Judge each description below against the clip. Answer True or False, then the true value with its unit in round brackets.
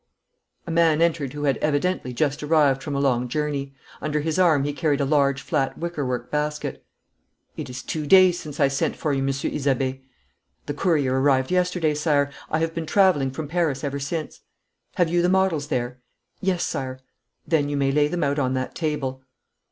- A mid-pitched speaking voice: True (145 Hz)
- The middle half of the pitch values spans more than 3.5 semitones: False (2.9 semitones)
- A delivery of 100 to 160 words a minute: False (190 wpm)